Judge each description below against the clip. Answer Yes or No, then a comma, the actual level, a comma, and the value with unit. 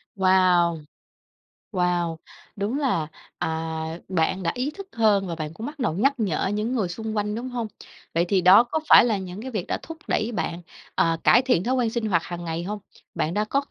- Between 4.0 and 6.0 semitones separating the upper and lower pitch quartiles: Yes, average, 5.1 semitones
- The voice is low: No, high, 205 Hz